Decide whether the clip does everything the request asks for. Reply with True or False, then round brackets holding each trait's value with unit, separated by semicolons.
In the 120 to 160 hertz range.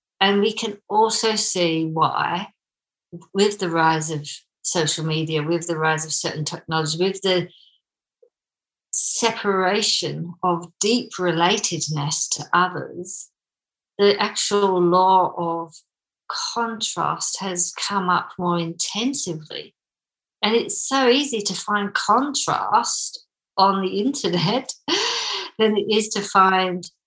False (185 Hz)